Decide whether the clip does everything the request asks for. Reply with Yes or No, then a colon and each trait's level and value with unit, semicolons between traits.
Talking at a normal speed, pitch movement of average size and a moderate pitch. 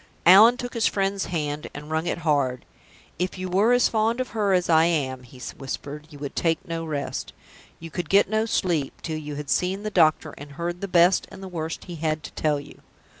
No: fast, 225 wpm; average, 4.4 semitones; medium, 165 Hz